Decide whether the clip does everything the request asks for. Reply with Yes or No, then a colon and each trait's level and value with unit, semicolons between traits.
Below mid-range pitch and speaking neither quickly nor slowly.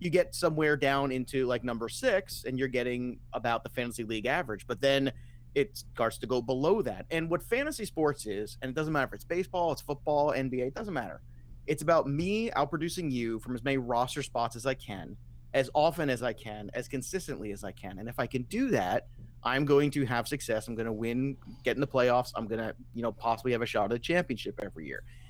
No: low, 125 Hz; fast, 230 wpm